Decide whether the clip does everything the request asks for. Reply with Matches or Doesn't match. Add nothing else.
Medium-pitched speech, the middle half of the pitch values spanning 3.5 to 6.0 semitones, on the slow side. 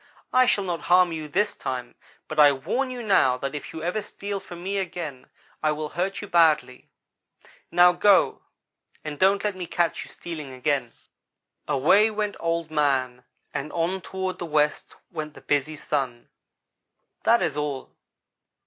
Doesn't match